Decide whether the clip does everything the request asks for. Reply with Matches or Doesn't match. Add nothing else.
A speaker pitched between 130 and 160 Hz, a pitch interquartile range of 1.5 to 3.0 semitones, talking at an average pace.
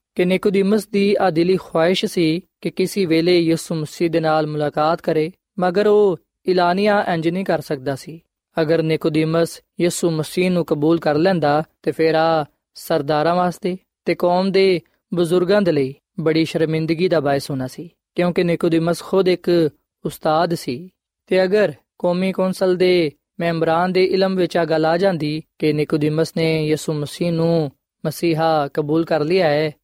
Doesn't match